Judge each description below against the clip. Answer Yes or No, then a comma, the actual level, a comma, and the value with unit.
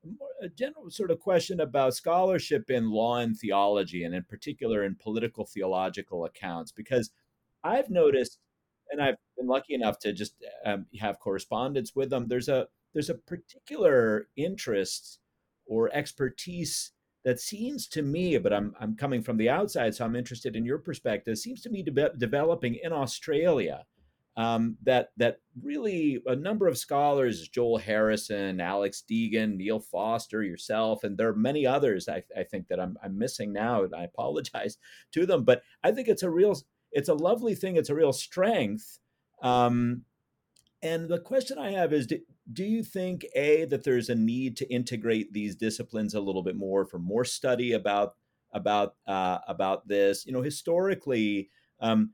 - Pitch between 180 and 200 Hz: No, low, 125 Hz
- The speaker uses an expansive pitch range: Yes, wide, 7.6 semitones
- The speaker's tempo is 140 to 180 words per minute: Yes, average, 170 wpm